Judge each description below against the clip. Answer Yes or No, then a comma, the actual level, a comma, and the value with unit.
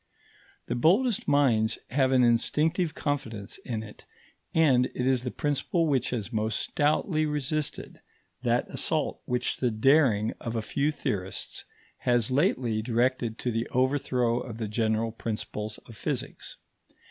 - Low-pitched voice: Yes, low, 125 Hz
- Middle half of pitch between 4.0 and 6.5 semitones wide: Yes, average, 4.3 semitones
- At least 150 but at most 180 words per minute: No, average, 140 wpm